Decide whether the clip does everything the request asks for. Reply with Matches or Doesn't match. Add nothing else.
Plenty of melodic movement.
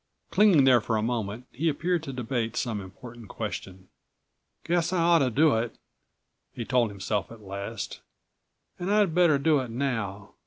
Matches